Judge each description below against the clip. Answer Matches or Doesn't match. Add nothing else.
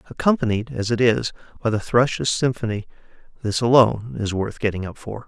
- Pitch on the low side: Matches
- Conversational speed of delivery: Matches